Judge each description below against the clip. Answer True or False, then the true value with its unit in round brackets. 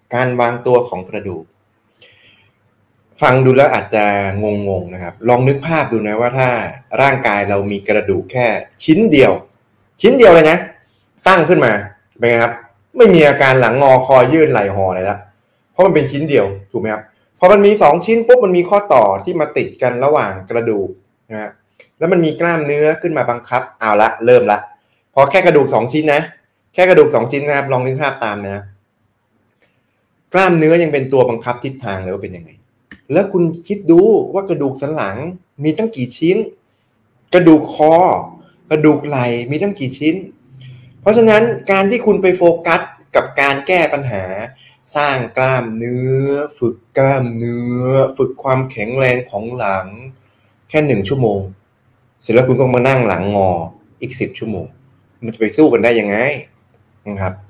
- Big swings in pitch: True (5.8 semitones)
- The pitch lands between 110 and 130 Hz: True (125 Hz)